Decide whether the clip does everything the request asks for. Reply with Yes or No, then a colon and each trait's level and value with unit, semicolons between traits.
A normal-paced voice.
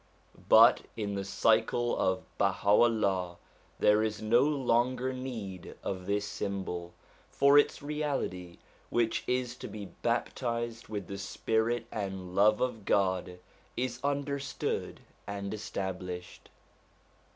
No: slow, 120 wpm